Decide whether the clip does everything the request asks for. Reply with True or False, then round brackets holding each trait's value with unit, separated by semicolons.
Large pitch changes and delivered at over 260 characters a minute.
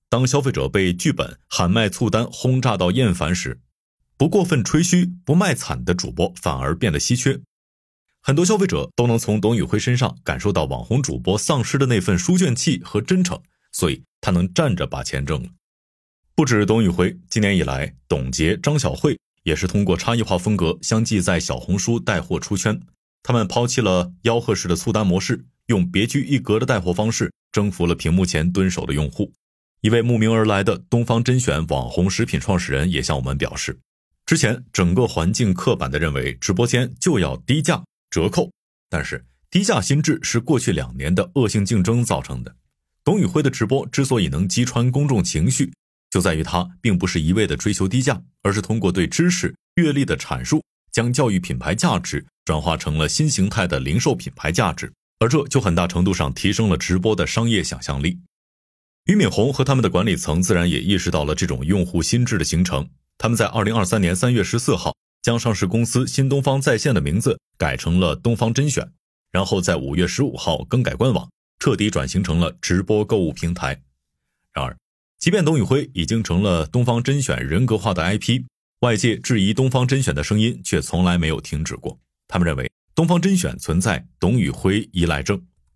True (6.3 semitones; 300 characters per minute)